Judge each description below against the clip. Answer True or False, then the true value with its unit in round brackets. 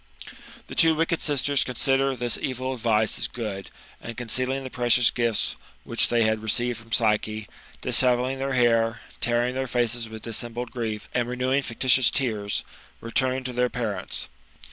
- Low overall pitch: True (120 Hz)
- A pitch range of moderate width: False (2.3 semitones)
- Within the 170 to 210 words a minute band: False (160 wpm)